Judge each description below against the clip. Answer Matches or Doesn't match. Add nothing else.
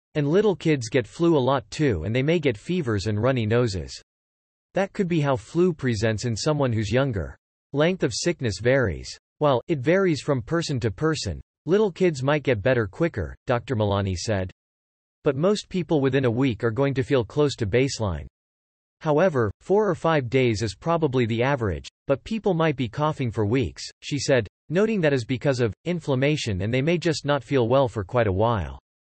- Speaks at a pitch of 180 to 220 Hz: Doesn't match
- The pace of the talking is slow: Doesn't match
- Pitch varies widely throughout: Matches